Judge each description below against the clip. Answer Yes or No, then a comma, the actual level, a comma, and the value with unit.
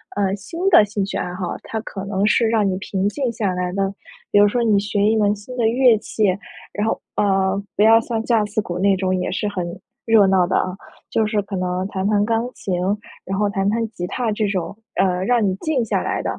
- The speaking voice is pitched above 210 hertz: No, high, 205 Hz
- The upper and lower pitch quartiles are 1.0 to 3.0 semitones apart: Yes, narrow, 2.5 semitones